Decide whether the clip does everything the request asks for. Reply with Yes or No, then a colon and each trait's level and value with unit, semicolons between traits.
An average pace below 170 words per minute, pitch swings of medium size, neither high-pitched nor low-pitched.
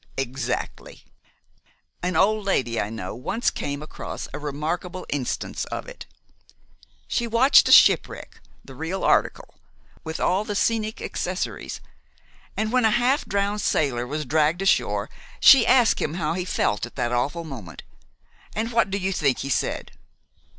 No: average, 155 wpm; wide, 7.7 semitones; medium, 170 Hz